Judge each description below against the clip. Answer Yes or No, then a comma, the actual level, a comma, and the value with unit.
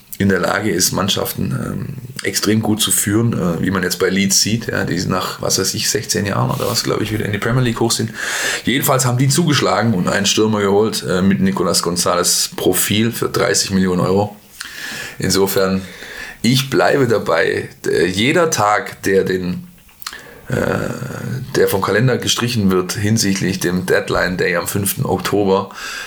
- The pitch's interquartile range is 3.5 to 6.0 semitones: No, average, 3.1 semitones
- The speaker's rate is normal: Yes, average, 175 wpm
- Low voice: Yes, low, 100 Hz